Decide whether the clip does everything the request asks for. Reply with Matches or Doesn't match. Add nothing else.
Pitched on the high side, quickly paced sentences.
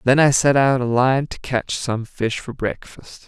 Doesn't match